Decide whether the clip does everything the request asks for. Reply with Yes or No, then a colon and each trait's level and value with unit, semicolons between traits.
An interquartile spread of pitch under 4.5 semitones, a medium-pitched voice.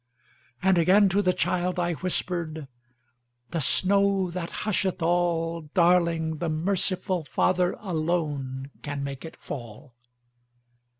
Yes: average, 3.8 semitones; medium, 170 Hz